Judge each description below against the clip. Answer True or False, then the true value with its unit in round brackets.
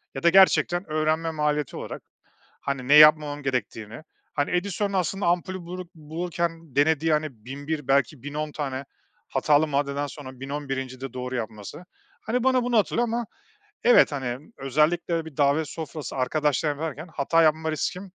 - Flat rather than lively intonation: False (3.4 semitones)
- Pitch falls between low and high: True (150 Hz)